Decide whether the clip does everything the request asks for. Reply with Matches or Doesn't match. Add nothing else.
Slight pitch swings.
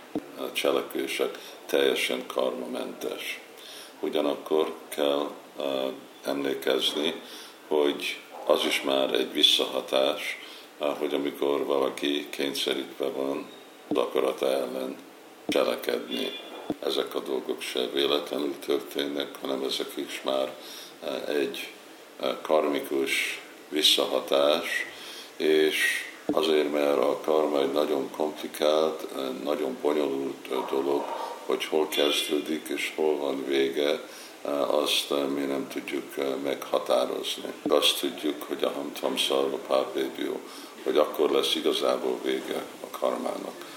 Matches